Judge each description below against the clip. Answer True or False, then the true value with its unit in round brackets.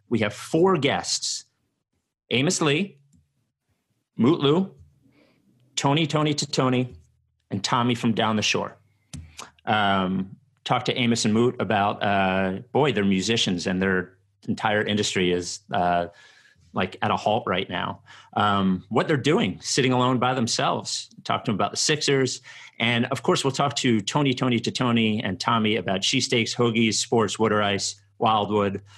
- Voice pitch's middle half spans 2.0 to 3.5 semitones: False (4.5 semitones)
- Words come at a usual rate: True (155 wpm)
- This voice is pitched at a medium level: False (115 Hz)